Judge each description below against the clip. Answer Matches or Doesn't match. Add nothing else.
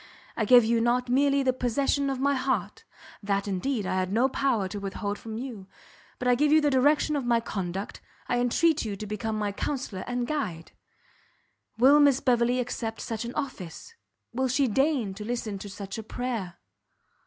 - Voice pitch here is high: Matches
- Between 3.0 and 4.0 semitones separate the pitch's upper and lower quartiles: Doesn't match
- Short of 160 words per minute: Doesn't match